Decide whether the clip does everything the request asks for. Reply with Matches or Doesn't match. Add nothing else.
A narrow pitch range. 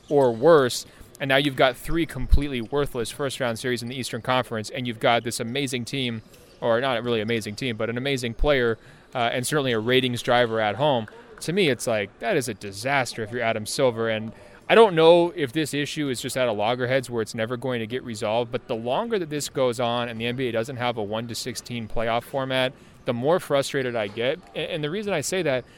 Doesn't match